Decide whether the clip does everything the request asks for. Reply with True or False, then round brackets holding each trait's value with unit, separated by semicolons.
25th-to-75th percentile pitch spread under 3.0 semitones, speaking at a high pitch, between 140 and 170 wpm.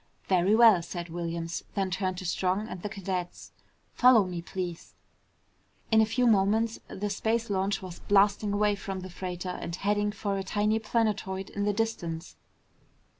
True (2.5 semitones; 195 Hz; 165 wpm)